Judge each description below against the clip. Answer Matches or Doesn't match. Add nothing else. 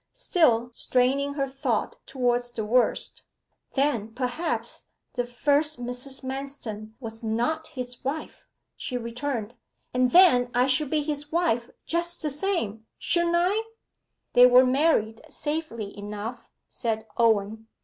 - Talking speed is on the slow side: Matches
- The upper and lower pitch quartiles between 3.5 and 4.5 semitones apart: Matches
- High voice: Matches